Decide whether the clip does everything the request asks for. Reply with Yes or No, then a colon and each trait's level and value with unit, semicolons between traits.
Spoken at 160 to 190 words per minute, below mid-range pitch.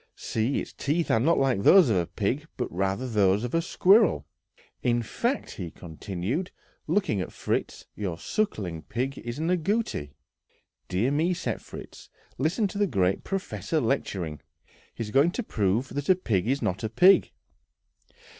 Yes: average, 165 wpm; low, 125 Hz